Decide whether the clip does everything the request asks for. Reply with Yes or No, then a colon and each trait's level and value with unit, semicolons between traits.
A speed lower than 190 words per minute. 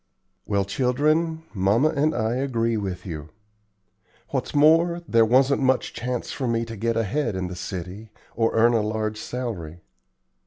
Yes: average, 155 wpm